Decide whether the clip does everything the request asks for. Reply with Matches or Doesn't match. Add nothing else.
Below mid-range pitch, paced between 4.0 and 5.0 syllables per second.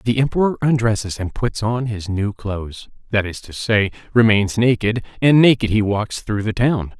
Matches